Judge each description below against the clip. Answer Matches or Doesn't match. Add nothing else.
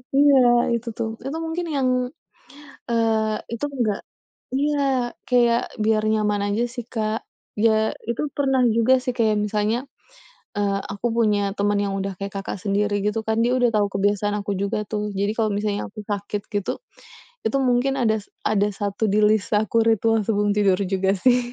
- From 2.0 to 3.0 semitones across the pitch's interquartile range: Matches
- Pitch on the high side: Matches